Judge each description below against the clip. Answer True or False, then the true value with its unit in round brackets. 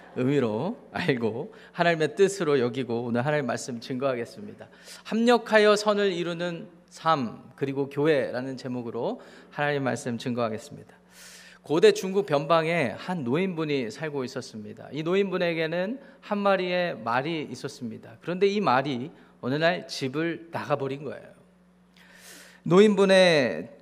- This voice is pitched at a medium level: True (160 Hz)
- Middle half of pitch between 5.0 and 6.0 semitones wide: True (5.5 semitones)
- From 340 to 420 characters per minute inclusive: False (310 characters per minute)